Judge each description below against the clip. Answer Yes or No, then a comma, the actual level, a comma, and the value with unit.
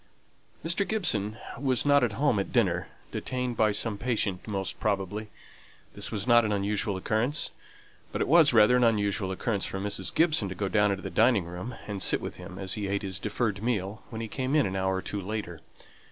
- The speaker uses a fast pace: Yes, fast, 210 wpm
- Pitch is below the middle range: Yes, low, 105 Hz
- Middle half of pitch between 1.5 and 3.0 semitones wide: No, average, 3.8 semitones